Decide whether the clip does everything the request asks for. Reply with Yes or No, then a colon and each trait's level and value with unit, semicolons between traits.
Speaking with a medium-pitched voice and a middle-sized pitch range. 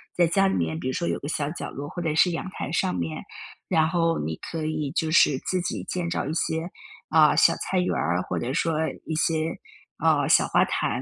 Yes: medium, 160 Hz; average, 3.4 semitones